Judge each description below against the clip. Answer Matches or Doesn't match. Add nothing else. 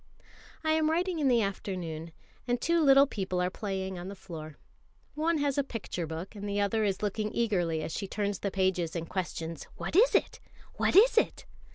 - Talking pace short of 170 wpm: Doesn't match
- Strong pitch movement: Matches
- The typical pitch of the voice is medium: Doesn't match